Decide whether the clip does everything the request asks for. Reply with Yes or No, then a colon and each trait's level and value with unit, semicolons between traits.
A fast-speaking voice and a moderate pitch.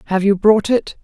No: fast, 230 wpm; high, 205 Hz